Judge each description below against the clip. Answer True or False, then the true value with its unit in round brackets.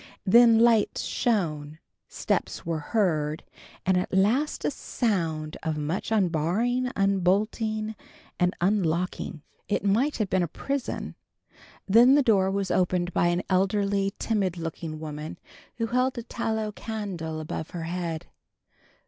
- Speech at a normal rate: False (130 wpm)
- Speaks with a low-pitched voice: False (190 Hz)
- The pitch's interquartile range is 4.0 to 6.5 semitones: True (4.8 semitones)